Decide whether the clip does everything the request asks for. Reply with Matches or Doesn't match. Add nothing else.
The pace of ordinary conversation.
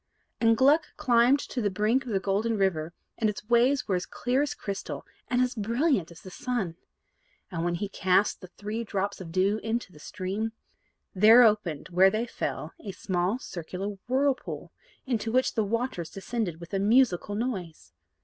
Matches